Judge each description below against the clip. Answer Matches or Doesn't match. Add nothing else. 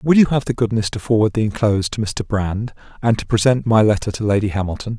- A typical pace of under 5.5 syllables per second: Doesn't match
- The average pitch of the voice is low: Matches